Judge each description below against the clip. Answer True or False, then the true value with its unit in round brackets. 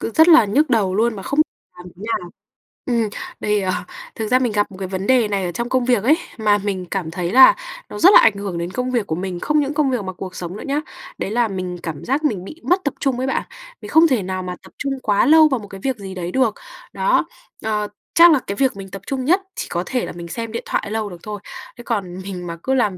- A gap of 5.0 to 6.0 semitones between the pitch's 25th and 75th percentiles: True (5.6 semitones)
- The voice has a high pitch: True (215 Hz)